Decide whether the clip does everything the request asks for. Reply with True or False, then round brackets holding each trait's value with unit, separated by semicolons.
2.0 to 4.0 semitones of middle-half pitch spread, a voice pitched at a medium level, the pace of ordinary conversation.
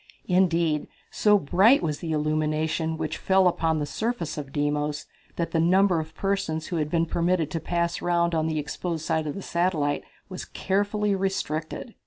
True (3.0 semitones; 165 Hz; 175 wpm)